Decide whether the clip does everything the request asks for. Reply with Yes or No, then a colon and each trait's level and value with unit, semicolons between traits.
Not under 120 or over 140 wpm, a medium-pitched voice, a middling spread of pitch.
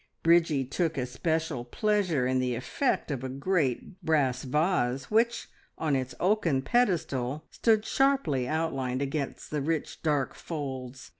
Yes: slow, 135 wpm; medium, 150 Hz; average, 4.9 semitones